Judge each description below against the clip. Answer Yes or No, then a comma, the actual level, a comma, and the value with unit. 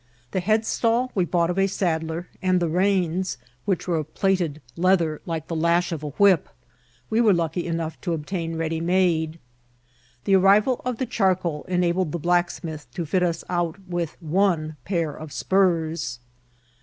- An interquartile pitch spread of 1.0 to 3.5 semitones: Yes, average, 2.7 semitones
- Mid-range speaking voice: Yes, medium, 175 Hz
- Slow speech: No, average, 165 wpm